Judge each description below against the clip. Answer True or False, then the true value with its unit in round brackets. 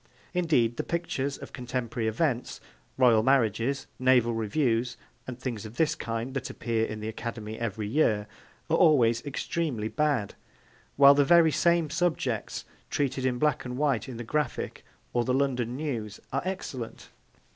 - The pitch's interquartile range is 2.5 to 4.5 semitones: True (4.1 semitones)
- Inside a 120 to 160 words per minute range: True (155 wpm)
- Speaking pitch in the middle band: False (125 Hz)